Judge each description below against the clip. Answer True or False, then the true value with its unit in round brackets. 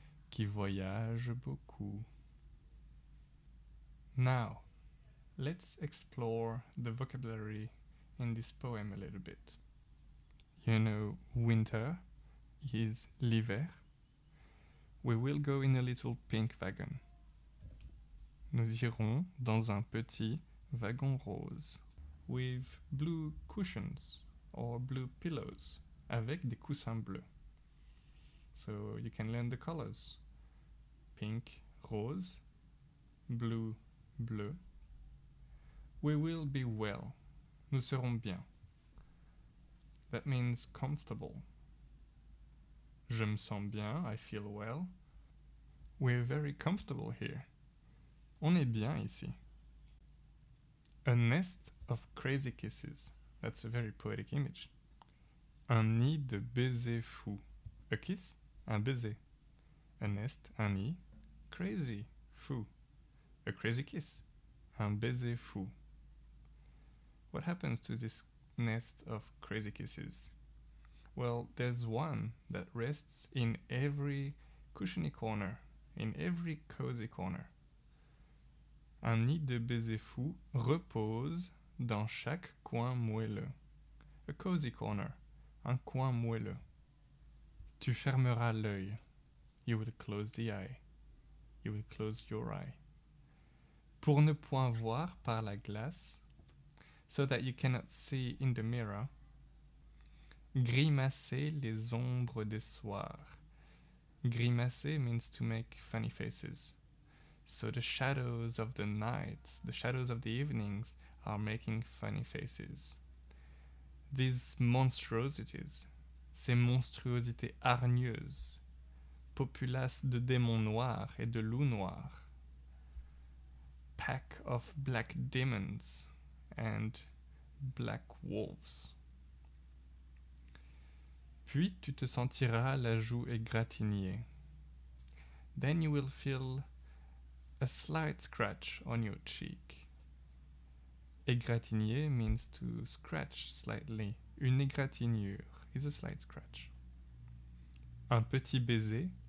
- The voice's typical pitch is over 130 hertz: False (115 Hz)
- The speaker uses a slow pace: True (100 wpm)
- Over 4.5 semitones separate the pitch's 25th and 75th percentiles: True (5.3 semitones)